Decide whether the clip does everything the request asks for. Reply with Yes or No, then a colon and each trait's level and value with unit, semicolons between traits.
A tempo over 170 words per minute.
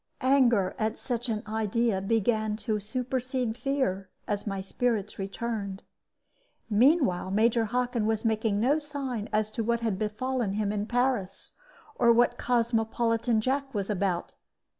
No: average, 140 wpm